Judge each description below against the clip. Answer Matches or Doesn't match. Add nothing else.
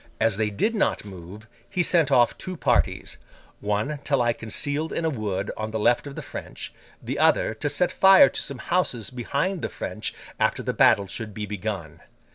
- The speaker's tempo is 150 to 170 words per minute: Doesn't match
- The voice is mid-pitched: Doesn't match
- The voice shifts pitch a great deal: Matches